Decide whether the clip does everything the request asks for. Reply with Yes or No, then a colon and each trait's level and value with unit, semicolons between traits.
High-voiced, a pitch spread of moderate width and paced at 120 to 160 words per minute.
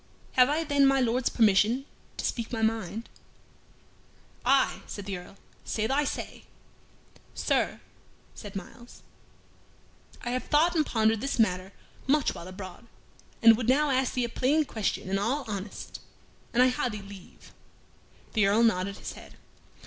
Yes: high, 230 Hz; average, 4.5 semitones; average, 155 wpm